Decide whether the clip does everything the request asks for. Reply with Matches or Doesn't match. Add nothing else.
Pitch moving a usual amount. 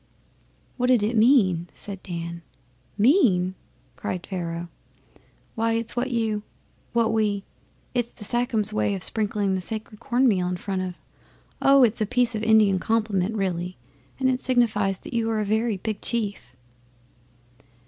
Matches